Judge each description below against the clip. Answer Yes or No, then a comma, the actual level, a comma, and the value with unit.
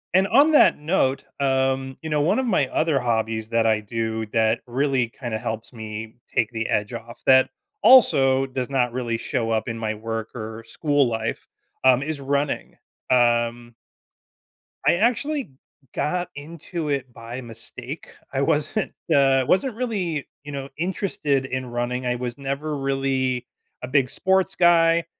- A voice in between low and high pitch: No, low, 130 Hz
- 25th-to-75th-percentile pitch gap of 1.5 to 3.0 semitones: No, average, 4.4 semitones